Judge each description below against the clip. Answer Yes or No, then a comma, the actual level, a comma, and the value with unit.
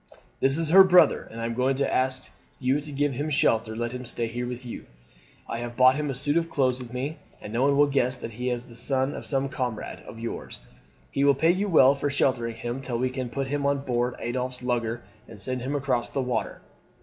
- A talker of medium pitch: No, low, 130 Hz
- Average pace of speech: No, fast, 250 wpm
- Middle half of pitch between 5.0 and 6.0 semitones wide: No, narrow, 2.6 semitones